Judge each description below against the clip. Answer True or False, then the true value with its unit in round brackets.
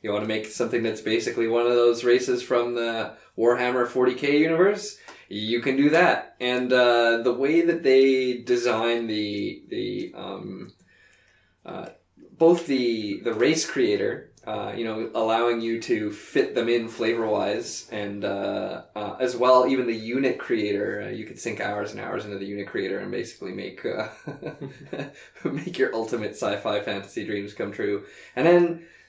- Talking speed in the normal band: True (170 wpm)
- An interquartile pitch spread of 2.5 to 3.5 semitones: True (3.0 semitones)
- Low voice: True (120 Hz)